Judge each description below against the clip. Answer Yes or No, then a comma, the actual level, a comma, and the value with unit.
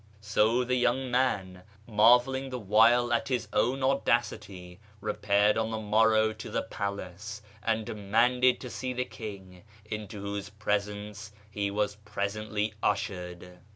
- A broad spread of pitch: No, average, 2.8 semitones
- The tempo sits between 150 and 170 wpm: No, average, 140 wpm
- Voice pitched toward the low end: Yes, low, 105 Hz